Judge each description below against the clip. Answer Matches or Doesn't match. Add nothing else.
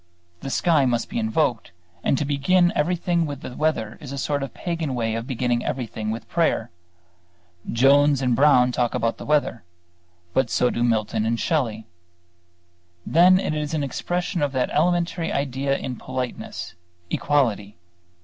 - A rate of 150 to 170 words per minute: Matches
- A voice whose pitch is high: Doesn't match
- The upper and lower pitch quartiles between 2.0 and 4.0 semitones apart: Doesn't match